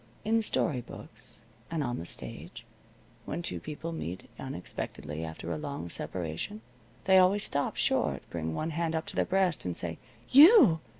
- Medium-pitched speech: Yes, medium, 150 Hz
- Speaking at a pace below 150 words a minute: No, average, 165 wpm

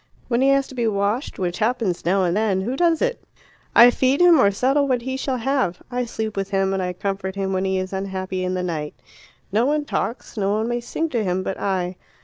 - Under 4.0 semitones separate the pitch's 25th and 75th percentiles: No, average, 5.2 semitones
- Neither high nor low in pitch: No, high, 210 Hz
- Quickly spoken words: Yes, fast, 240 wpm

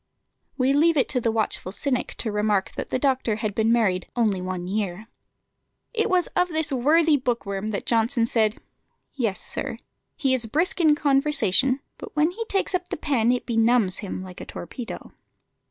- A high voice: Yes, high, 240 Hz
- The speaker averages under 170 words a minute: No, average, 185 wpm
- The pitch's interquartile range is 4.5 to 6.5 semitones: Yes, wide, 5.6 semitones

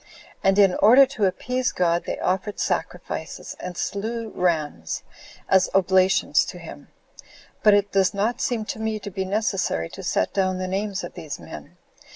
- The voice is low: No, high, 195 Hz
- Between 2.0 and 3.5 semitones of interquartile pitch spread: Yes, average, 2.7 semitones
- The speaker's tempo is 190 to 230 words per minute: No, average, 170 wpm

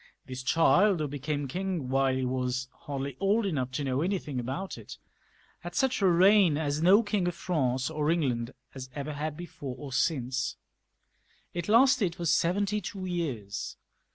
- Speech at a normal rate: Yes, average, 165 wpm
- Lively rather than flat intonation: Yes, wide, 5.9 semitones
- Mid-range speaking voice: Yes, medium, 150 Hz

